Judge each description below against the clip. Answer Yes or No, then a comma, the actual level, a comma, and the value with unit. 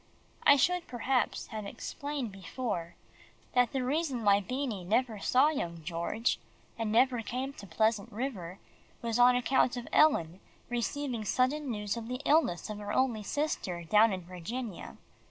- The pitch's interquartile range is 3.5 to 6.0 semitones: Yes, average, 4.5 semitones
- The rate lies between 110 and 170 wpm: Yes, average, 155 wpm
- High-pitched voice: Yes, high, 235 Hz